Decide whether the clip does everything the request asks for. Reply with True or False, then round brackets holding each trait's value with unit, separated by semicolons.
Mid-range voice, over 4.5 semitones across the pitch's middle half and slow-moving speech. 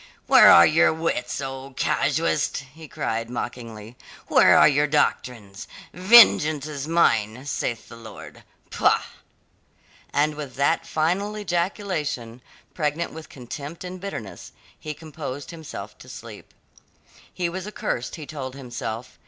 True (145 Hz; 5.0 semitones; 130 wpm)